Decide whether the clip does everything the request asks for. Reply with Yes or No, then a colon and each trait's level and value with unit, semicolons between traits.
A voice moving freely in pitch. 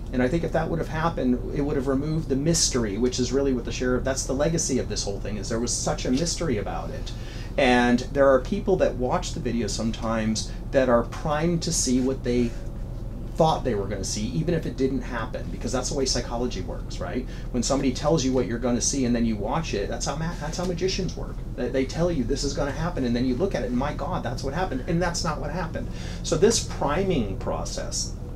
No: average, 3.4 semitones